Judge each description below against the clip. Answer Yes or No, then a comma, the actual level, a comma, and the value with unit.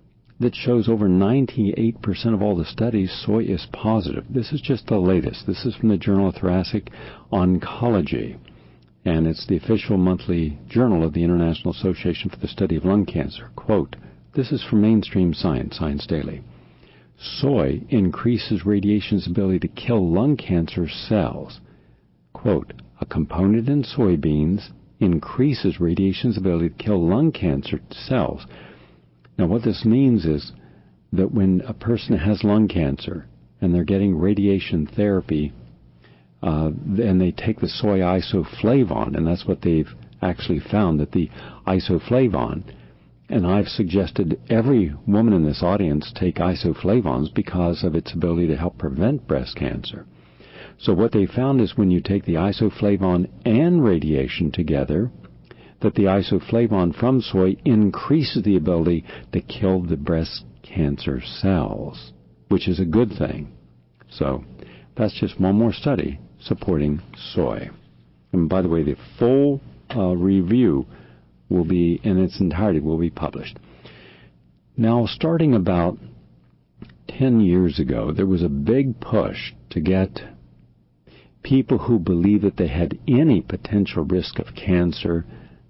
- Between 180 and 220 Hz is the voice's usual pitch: No, very low, 90 Hz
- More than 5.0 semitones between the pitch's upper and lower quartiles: Yes, wide, 5.4 semitones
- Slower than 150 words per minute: Yes, average, 140 wpm